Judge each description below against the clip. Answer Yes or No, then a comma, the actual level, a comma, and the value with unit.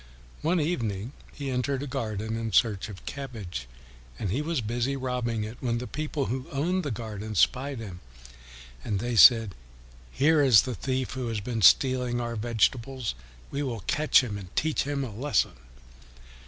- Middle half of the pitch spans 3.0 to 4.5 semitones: Yes, average, 3.9 semitones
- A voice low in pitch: Yes, low, 120 Hz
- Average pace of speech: Yes, average, 170 wpm